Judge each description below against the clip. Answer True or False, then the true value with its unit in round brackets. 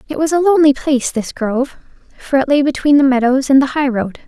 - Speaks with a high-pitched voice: True (275 Hz)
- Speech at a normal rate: False (240 wpm)